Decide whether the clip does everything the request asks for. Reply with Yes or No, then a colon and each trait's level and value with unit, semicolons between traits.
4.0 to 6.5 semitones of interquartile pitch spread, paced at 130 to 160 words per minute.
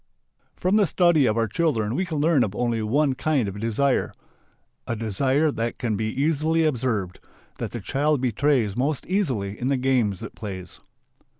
No: wide, 5.6 semitones; average, 175 wpm